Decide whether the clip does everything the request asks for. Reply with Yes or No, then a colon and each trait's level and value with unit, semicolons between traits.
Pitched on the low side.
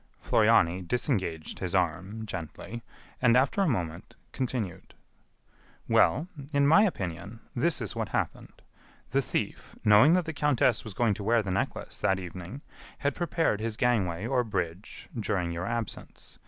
Yes: low, 110 Hz